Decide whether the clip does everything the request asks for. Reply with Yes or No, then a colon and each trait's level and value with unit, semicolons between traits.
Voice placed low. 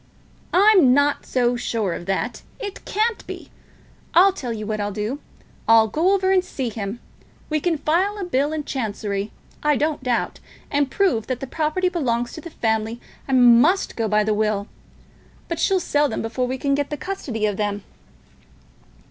No: very high, 260 Hz